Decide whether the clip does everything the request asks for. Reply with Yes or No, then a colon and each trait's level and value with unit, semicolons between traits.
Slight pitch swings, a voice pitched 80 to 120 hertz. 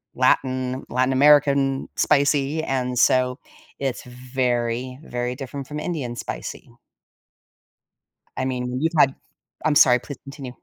No: narrow, 1.8 semitones; low, 130 Hz